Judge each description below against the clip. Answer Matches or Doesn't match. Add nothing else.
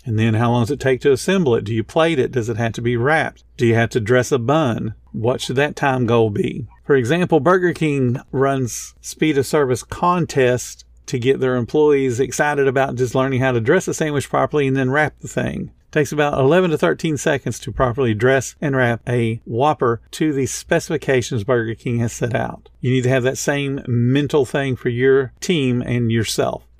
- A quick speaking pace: Matches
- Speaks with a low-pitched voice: Matches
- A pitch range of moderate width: Matches